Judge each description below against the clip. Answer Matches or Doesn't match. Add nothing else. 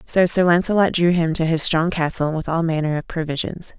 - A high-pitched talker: Doesn't match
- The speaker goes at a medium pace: Doesn't match